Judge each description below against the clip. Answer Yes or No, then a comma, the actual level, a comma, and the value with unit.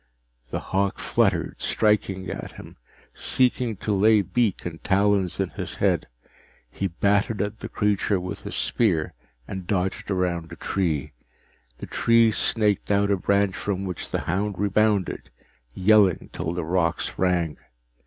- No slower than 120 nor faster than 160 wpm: Yes, average, 145 wpm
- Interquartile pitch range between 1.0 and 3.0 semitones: Yes, narrow, 2.4 semitones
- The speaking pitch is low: Yes, very low, 95 Hz